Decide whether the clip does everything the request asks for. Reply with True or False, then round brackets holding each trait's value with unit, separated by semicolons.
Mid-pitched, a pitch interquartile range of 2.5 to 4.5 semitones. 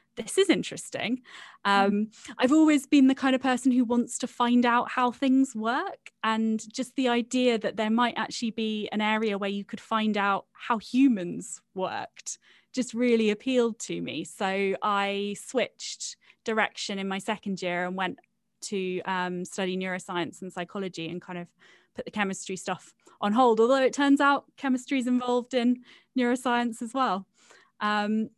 False (225 Hz; 4.0 semitones)